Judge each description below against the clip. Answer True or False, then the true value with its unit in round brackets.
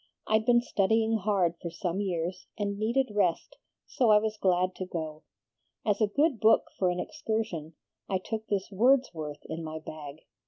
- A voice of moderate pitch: False (200 Hz)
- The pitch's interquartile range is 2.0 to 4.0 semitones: False (4.4 semitones)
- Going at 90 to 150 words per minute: False (170 wpm)